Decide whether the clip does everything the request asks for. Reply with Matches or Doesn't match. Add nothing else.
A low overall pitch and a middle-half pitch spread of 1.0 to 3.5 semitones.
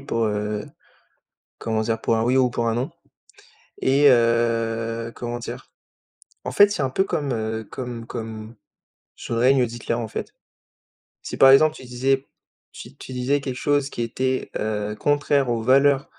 Matches